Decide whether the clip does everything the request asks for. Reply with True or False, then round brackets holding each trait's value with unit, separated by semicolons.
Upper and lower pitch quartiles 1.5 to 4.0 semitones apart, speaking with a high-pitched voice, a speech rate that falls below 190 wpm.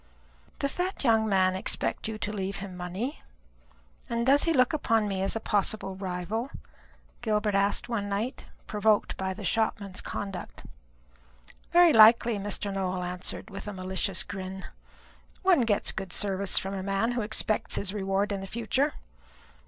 True (2.9 semitones; 205 Hz; 160 wpm)